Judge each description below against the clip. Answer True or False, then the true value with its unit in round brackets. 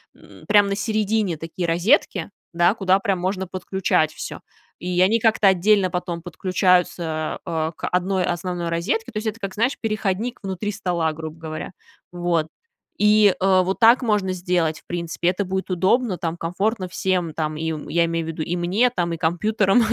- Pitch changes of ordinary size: True (3.3 semitones)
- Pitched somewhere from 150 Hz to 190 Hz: True (185 Hz)